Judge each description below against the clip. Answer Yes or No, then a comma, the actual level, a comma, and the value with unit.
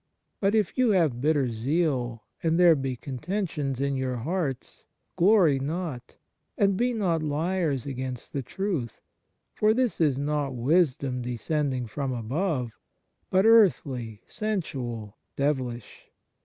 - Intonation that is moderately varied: No, wide, 6.1 semitones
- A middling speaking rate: No, slow, 125 wpm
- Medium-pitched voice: Yes, medium, 145 Hz